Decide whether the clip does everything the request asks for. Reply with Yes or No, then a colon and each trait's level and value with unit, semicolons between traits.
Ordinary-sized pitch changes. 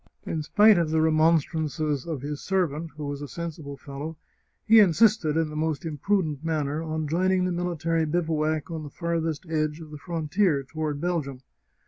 No: narrow, 2.1 semitones